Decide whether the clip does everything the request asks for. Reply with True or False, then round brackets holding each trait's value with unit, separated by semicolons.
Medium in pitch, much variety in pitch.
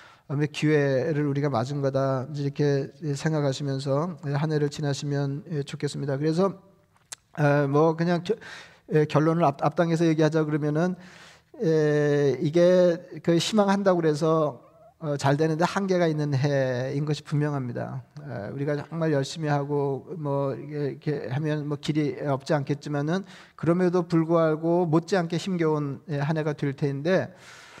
False (150 Hz; 2.7 semitones)